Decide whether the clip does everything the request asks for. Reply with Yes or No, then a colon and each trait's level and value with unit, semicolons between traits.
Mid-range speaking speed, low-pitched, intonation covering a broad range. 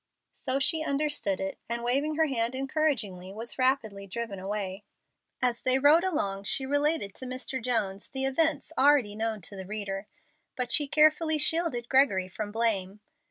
No: average, 160 wpm; high, 240 Hz; wide, 5.9 semitones